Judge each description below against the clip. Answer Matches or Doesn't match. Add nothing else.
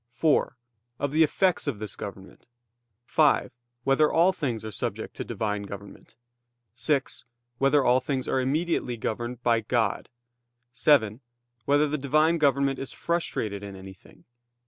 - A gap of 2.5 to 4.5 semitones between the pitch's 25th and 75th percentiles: Doesn't match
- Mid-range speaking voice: Doesn't match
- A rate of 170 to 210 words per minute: Doesn't match